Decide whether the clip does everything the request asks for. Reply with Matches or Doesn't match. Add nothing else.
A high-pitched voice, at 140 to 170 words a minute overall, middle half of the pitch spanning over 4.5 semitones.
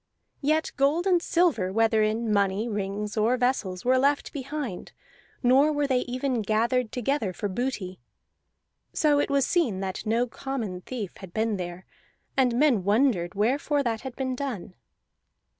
Matches